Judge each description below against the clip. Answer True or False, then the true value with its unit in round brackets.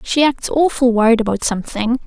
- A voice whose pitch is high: True (245 Hz)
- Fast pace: False (175 wpm)